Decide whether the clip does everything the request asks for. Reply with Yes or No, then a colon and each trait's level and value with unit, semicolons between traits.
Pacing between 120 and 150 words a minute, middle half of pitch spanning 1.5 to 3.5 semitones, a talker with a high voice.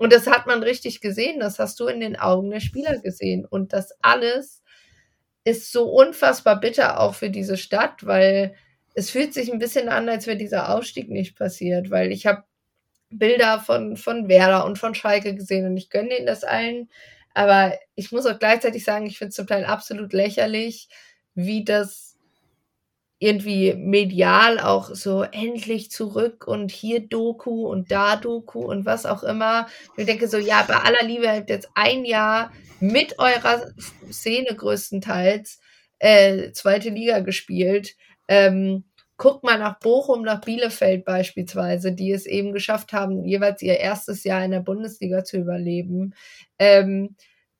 No: average, 165 wpm; average, 3.2 semitones; high, 210 Hz